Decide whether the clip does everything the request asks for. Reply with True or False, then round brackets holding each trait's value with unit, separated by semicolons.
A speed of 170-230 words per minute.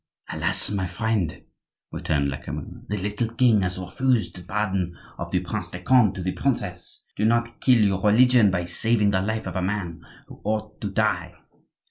True (180 wpm)